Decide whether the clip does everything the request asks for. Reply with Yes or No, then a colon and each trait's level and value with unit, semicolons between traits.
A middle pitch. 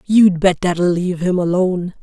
Yes: medium, 180 Hz